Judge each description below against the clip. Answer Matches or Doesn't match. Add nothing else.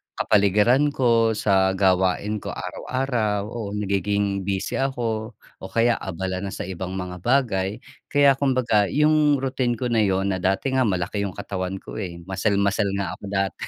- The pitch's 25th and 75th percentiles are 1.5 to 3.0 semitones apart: Doesn't match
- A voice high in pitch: Doesn't match